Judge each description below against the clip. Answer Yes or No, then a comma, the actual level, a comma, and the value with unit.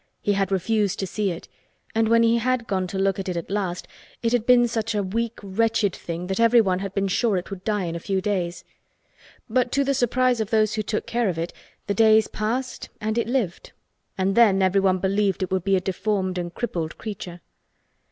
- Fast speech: Yes, fast, 220 wpm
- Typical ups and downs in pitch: Yes, average, 3.4 semitones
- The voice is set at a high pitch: Yes, high, 200 Hz